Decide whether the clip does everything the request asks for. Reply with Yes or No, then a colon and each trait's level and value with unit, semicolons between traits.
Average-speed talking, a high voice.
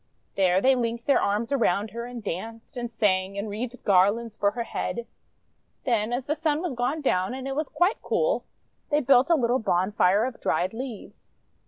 Yes: average, 190 wpm; high, 235 Hz